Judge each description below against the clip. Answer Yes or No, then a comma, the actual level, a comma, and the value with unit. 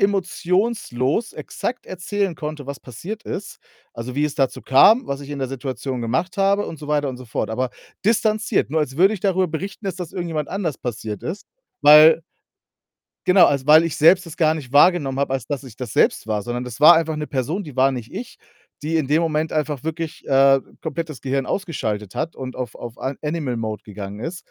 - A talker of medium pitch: Yes, medium, 150 Hz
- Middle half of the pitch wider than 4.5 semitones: Yes, average, 5.1 semitones